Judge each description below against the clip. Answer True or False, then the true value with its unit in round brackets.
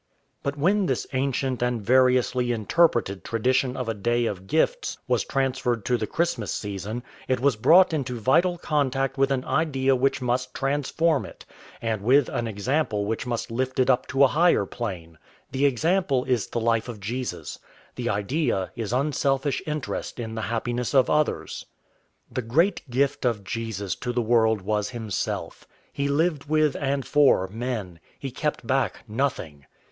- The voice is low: True (125 Hz)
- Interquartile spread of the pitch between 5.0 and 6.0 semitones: False (3.7 semitones)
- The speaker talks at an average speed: True (165 wpm)